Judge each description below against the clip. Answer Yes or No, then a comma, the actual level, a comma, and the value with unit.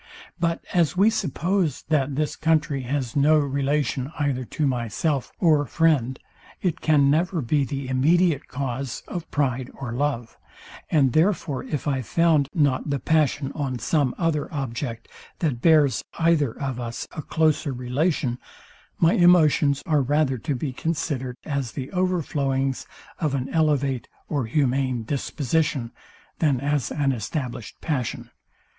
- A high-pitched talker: No, medium, 145 Hz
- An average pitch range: Yes, average, 3.3 semitones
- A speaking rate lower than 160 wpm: Yes, average, 140 wpm